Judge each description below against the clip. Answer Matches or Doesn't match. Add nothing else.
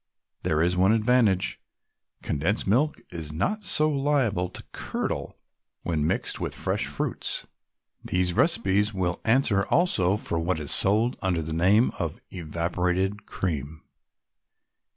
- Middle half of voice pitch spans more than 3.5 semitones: Matches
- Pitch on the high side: Doesn't match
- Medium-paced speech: Doesn't match